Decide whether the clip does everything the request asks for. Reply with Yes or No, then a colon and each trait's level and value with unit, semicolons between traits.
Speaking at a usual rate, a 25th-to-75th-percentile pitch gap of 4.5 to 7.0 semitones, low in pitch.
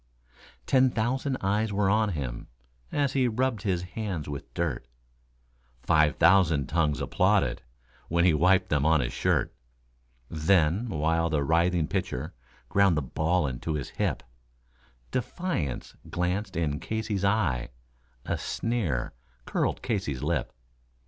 No: slow, 130 wpm; wide, 5.6 semitones; very low, 85 Hz